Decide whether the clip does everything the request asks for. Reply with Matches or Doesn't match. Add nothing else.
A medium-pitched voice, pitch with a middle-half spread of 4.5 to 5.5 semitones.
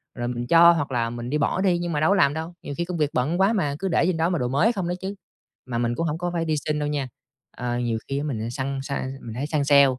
Matches